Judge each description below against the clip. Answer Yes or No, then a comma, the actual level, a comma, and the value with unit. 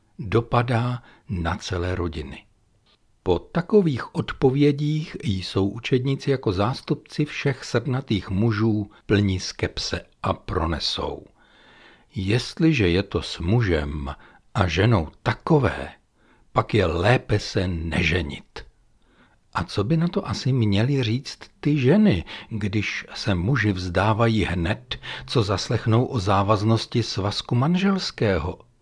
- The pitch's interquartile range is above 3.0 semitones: Yes, average, 5.1 semitones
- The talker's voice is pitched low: Yes, low, 110 Hz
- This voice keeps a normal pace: No, slow, 110 wpm